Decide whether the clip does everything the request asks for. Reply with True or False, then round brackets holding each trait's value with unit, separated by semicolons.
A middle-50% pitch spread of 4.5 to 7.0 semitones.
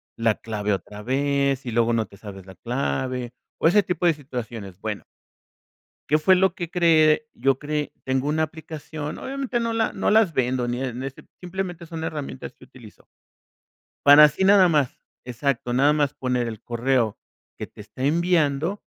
True (5.2 semitones)